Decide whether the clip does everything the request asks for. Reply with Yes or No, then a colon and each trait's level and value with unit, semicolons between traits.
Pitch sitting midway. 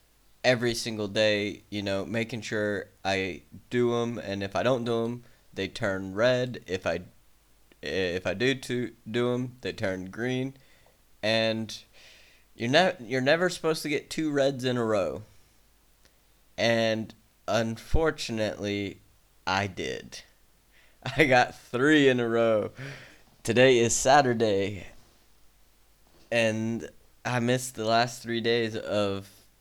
No: low, 115 Hz